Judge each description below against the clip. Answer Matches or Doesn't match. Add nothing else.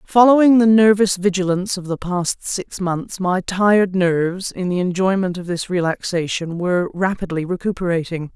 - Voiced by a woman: Matches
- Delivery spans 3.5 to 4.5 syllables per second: Doesn't match